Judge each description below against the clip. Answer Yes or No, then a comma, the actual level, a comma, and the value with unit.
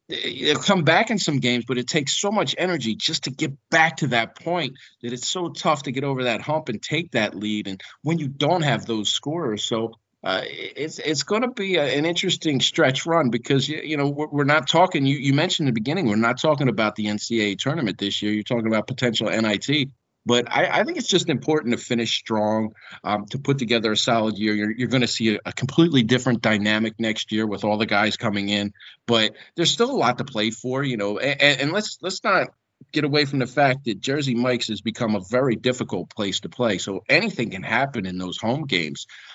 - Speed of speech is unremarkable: No, fast, 230 wpm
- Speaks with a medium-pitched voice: No, low, 125 Hz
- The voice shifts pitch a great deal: Yes, wide, 5.7 semitones